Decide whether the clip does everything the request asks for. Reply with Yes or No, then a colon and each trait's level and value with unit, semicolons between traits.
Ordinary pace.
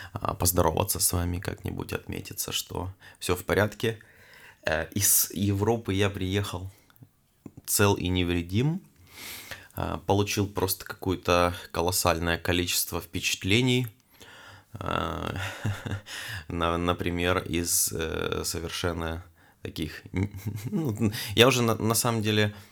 No: slow, 80 wpm